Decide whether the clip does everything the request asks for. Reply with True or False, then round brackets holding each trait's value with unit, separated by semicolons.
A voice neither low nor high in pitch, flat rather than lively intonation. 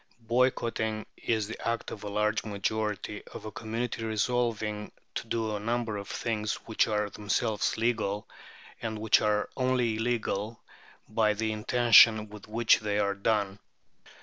False (110 Hz; 1.6 semitones)